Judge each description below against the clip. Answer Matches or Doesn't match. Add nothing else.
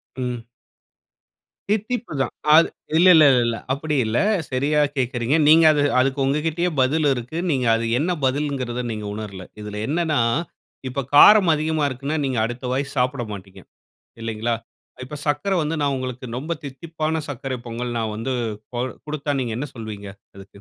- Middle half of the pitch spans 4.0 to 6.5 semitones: Matches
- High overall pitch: Doesn't match